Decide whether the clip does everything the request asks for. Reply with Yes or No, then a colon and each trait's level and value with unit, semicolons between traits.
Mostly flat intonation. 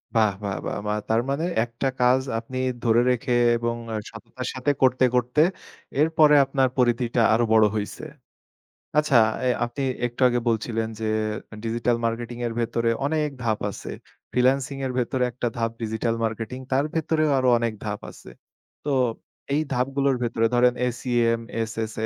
Yes: narrow, 2.3 semitones